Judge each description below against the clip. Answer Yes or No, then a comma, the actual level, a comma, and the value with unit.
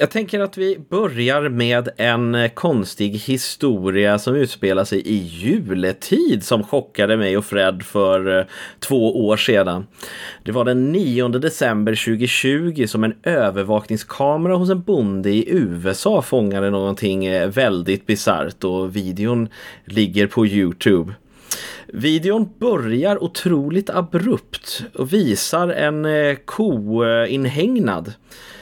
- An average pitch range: No, wide, 7.2 semitones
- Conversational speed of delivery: No, slow, 115 wpm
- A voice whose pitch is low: Yes, low, 115 Hz